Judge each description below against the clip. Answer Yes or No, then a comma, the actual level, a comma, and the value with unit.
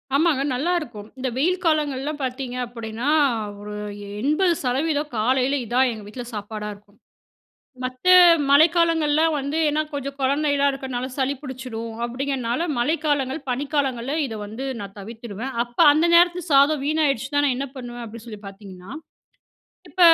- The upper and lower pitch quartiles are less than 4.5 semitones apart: Yes, average, 3.7 semitones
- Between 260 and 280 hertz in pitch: Yes, very high, 265 Hz